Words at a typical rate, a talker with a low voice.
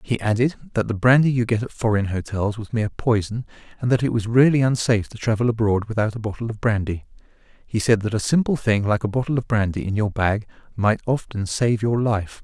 No: fast, 220 wpm; low, 110 Hz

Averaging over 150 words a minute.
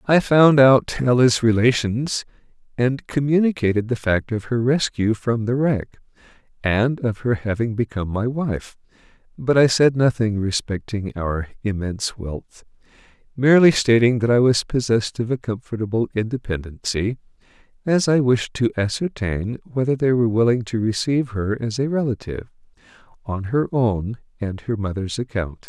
No: average, 145 wpm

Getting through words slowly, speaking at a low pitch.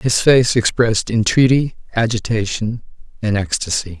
Yes: slow, 105 wpm; low, 110 Hz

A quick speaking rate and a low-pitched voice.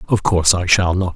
Yes: fast, 260 wpm; very low, 90 Hz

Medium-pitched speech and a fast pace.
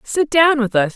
No: very high, 260 Hz; fast, 250 wpm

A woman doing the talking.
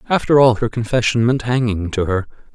No: male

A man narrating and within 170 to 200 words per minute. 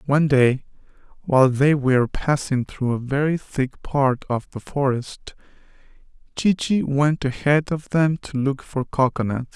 No: male; average, 150 wpm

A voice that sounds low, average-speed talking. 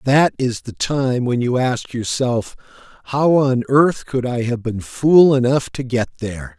Yes: low, 130 Hz; average, 180 wpm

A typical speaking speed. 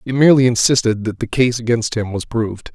No: fast, 220 wpm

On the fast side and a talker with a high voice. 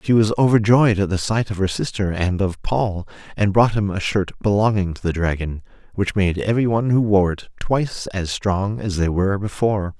No: fast, 210 wpm; low, 100 Hz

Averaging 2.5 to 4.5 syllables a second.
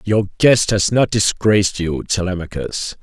Yes: 4.3 syllables/s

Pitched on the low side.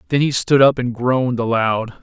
Yes: low, 125 Hz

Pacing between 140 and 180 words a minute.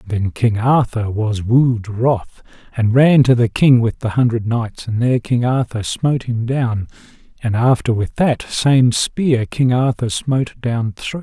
No: average, 190 wpm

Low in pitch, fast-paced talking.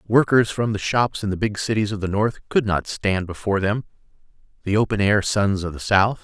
Yes: low, 100 Hz; fast, 220 wpm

